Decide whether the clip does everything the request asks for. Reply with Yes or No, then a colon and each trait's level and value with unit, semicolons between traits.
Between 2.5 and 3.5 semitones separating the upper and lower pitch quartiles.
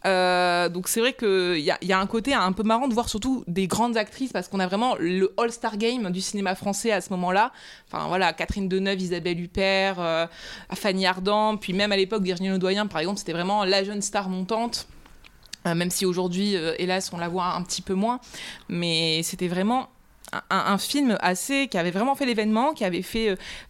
Yes: average, 3.2 semitones